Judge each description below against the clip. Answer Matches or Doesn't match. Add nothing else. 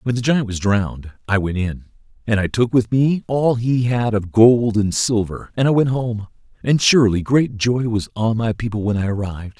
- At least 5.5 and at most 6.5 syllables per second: Doesn't match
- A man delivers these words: Matches